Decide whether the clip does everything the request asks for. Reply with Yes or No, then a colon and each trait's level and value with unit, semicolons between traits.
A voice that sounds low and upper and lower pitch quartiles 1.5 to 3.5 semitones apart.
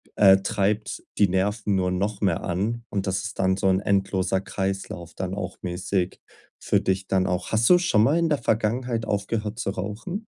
Yes: low, 100 Hz; average, 2.7 semitones